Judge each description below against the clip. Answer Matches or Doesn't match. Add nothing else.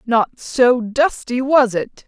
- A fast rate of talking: Doesn't match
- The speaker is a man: Doesn't match